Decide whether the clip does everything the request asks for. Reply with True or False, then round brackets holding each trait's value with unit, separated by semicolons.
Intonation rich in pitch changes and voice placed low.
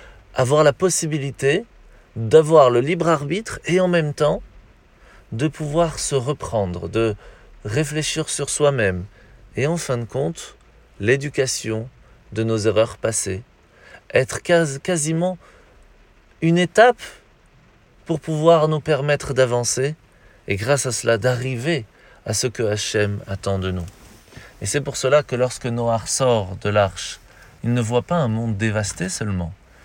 True (6.4 semitones; 125 Hz)